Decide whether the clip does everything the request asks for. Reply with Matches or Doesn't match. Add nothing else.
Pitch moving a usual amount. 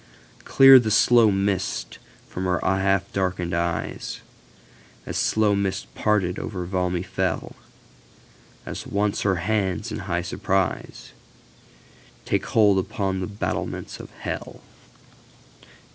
Doesn't match